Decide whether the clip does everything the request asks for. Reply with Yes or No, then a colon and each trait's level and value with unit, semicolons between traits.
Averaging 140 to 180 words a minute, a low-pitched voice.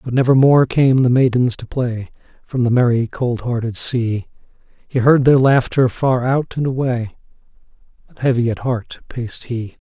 Yes: average, 170 wpm; low, 125 Hz